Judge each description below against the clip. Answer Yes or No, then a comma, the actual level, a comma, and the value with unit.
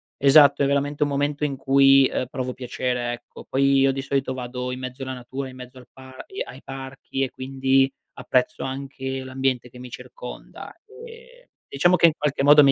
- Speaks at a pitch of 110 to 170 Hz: Yes, low, 135 Hz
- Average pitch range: No, narrow, 1.5 semitones